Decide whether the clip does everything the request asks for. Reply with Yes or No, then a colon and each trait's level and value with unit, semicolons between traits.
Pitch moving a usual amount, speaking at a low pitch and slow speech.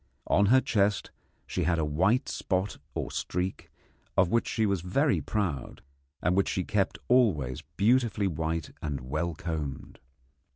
No: average, 4.9 semitones; very low, 90 Hz; average, 150 wpm